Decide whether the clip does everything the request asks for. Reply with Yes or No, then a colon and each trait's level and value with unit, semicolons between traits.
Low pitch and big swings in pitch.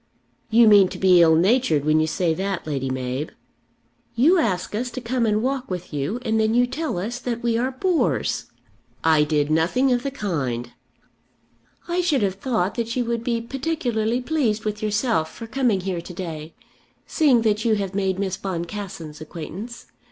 No: high, 210 Hz; wide, 6.2 semitones